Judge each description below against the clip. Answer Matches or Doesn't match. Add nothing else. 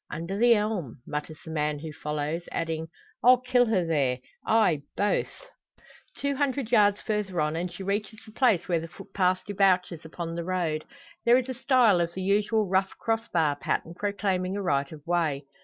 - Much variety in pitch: Doesn't match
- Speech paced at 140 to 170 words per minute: Doesn't match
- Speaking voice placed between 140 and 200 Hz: Matches